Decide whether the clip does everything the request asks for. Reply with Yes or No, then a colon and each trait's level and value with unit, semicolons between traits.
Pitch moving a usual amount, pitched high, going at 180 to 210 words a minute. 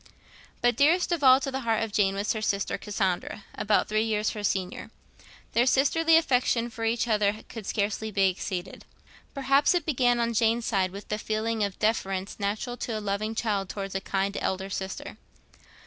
Yes: average, 3.3 semitones; high, 215 Hz; average, 185 wpm